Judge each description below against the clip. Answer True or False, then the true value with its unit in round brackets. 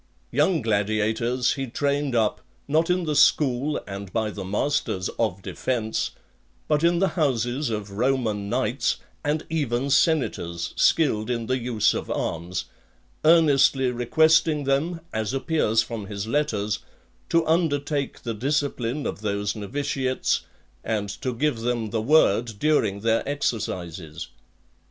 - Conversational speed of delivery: False (130 wpm)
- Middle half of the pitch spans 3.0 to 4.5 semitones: False (5.4 semitones)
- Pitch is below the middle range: True (125 Hz)